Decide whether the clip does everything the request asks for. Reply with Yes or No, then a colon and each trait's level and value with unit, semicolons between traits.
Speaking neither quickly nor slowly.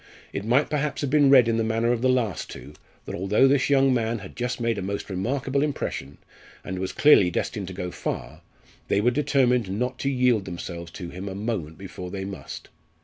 No: fast, 210 wpm